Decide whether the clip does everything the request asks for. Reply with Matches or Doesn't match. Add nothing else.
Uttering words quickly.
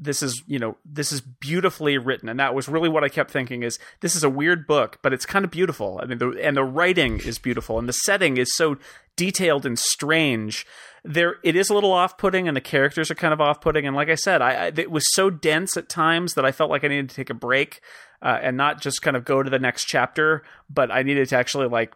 Matches